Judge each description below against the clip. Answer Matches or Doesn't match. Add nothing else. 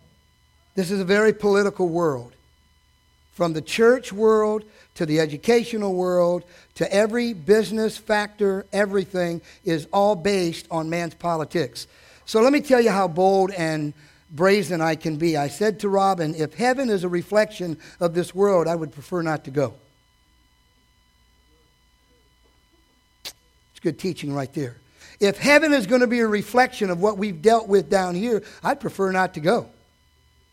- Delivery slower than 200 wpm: Matches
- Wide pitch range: Matches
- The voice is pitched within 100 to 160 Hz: Doesn't match